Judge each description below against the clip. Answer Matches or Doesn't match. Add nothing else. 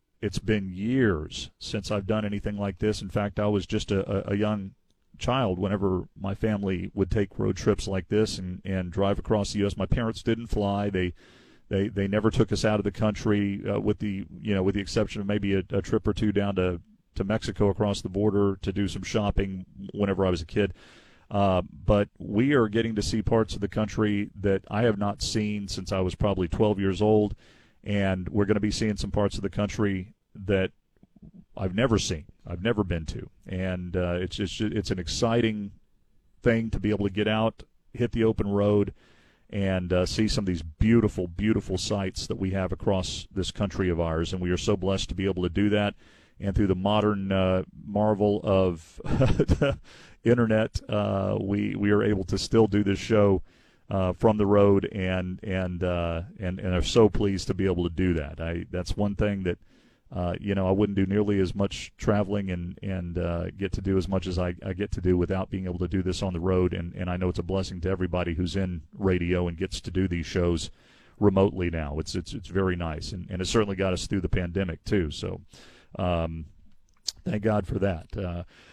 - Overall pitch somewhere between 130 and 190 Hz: Doesn't match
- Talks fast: Matches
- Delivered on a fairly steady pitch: Matches